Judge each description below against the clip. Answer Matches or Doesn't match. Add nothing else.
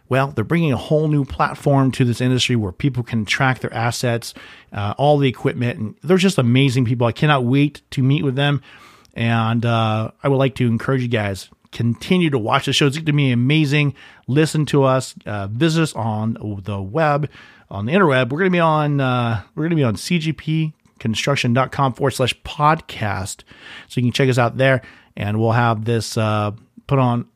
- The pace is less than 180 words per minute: Doesn't match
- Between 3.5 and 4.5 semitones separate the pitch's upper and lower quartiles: Matches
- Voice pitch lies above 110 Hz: Matches